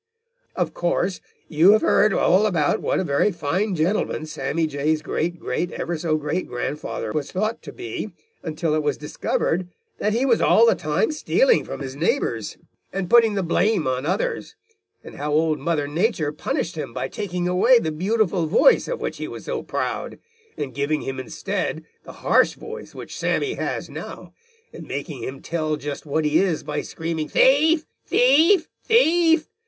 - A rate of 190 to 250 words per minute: No, average, 175 wpm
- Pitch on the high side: No, medium, 170 Hz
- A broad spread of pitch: Yes, wide, 6.3 semitones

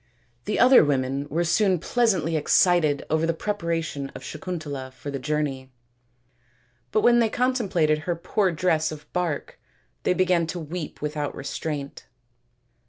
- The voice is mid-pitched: Yes, medium, 160 Hz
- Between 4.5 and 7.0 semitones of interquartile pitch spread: No, average, 3.8 semitones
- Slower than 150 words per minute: Yes, average, 140 wpm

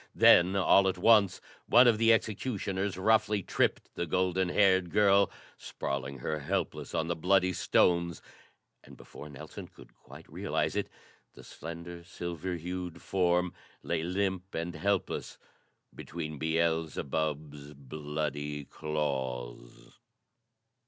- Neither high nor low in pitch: No, very low, 85 Hz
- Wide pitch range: No, average, 3.8 semitones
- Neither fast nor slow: No, slow, 120 wpm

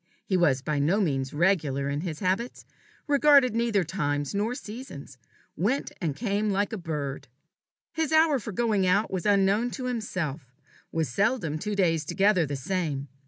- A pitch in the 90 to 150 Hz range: No, high, 190 Hz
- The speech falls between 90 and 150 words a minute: No, average, 165 wpm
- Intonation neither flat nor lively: No, wide, 6.6 semitones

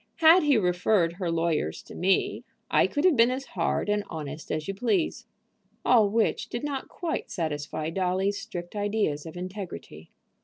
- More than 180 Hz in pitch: Yes, high, 190 Hz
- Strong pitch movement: Yes, wide, 5.8 semitones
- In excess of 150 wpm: Yes, average, 165 wpm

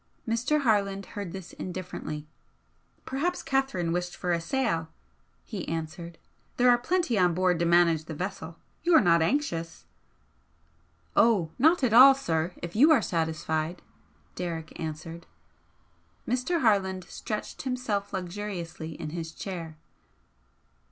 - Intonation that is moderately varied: No, wide, 6.1 semitones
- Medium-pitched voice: Yes, medium, 180 Hz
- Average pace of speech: No, slow, 125 wpm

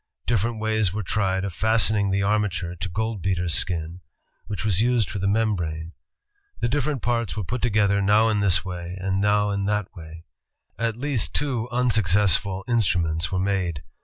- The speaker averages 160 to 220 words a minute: Yes, average, 170 wpm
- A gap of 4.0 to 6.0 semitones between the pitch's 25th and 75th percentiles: No, average, 3.3 semitones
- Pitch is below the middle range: Yes, low, 100 Hz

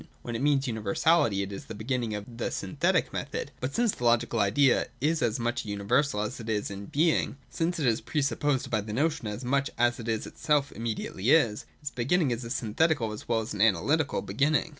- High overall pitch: No, low, 120 Hz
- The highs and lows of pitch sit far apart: No, average, 4.8 semitones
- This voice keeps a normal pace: No, fast, 220 wpm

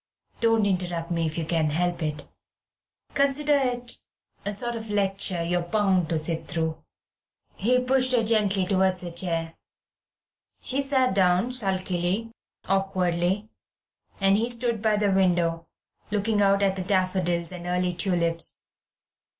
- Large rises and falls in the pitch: No, average, 4.0 semitones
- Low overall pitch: No, high, 190 Hz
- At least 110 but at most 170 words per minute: Yes, average, 140 wpm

